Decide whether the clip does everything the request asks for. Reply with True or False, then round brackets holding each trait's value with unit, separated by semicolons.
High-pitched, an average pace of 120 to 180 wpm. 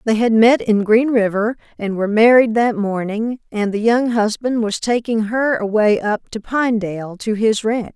False (220 Hz; 190 wpm)